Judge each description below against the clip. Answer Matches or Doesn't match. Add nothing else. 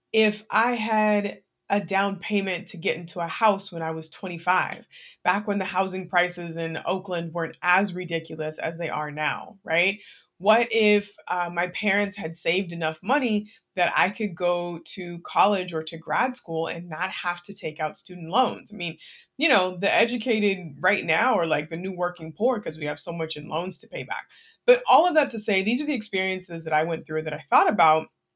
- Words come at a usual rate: Doesn't match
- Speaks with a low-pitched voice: Doesn't match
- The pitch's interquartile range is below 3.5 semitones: Doesn't match